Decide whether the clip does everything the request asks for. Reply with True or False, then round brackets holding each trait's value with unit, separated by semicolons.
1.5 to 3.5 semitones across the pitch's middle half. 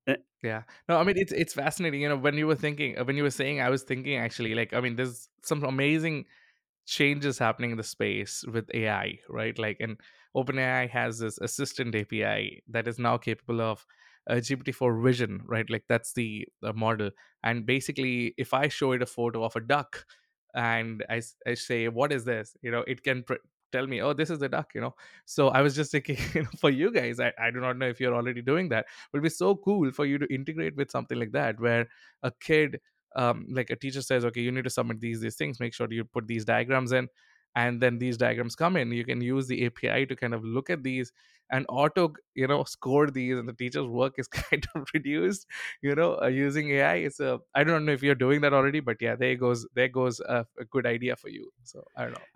True (3.2 semitones)